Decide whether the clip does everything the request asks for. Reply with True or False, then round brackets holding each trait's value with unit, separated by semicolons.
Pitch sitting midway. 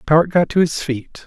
True (155 Hz)